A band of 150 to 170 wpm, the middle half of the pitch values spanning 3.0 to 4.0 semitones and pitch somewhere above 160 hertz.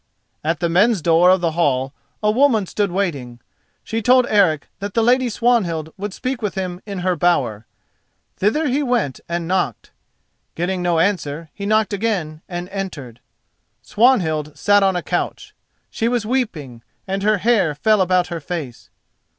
No: average, 165 wpm; average, 4.8 semitones; medium, 185 Hz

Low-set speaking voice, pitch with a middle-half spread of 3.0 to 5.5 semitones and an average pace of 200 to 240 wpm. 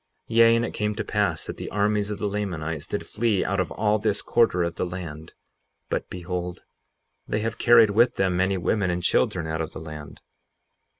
Yes: low, 100 Hz; average, 3.4 semitones; fast, 205 wpm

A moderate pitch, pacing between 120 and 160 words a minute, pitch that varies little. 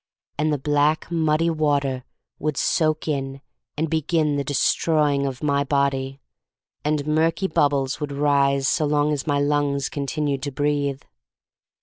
Yes: medium, 145 Hz; average, 150 wpm; narrow, 1.5 semitones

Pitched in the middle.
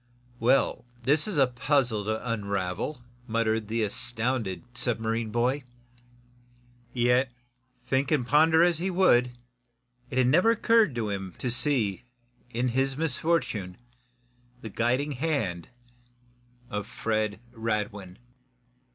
No: low, 120 Hz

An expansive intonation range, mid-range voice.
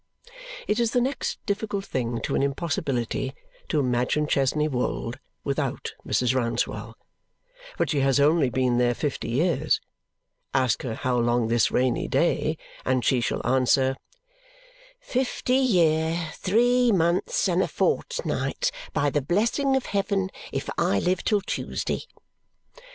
Yes: wide, 7.9 semitones; medium, 150 Hz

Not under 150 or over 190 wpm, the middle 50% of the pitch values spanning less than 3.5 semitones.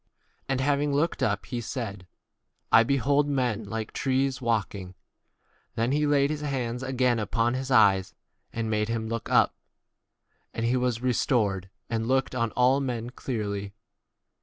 Yes: average, 165 wpm; average, 3.1 semitones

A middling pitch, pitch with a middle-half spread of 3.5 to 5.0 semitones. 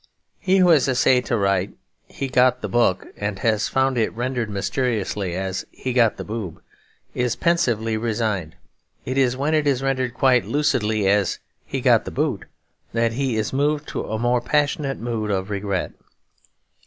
No: low, 120 Hz; average, 4.1 semitones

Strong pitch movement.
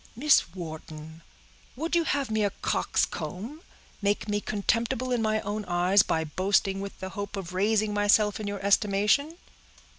No: average, 2.7 semitones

